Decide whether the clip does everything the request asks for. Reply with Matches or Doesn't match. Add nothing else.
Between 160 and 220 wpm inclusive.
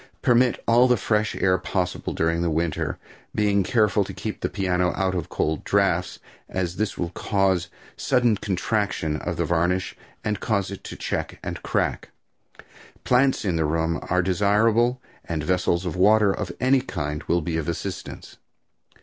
Matches